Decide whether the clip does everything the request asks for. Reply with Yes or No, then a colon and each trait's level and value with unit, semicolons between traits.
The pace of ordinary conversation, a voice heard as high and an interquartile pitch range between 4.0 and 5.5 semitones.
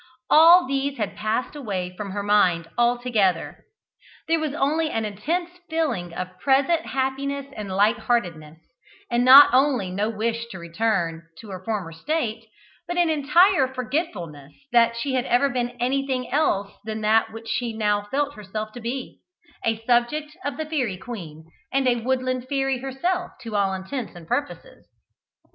Yes: average, 160 wpm; high, 240 Hz; average, 5.1 semitones